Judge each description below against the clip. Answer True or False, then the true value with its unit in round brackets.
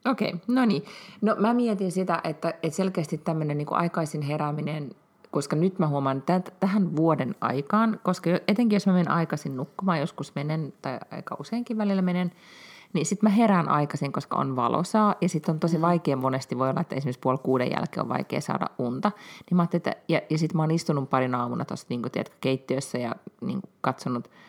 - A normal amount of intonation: True (5.0 semitones)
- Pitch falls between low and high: True (165 Hz)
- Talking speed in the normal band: False (200 wpm)